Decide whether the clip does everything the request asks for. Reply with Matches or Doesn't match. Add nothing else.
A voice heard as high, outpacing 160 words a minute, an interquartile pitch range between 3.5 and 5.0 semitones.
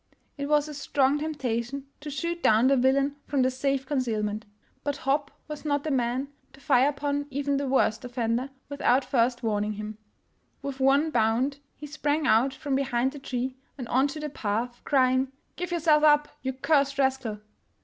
Doesn't match